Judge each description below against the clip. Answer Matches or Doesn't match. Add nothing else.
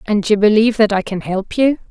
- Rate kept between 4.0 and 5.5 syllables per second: Doesn't match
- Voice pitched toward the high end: Matches